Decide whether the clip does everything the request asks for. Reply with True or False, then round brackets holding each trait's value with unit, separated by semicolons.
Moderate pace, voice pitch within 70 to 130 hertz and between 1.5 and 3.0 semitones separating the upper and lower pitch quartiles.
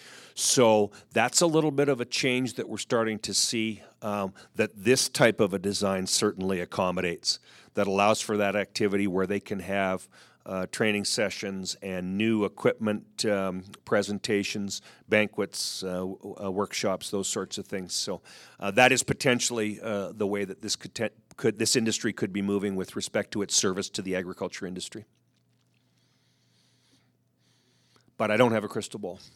True (170 wpm; 100 Hz; 2.6 semitones)